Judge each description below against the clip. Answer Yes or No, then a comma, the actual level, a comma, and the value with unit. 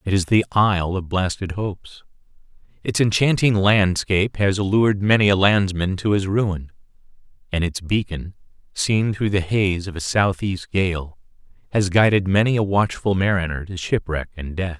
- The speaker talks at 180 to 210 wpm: No, average, 160 wpm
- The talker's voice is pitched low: Yes, very low, 95 Hz